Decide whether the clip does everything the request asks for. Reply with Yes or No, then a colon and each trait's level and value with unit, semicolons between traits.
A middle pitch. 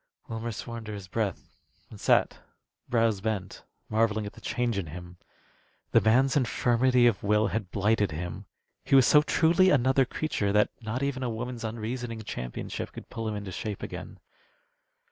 No: low, 110 Hz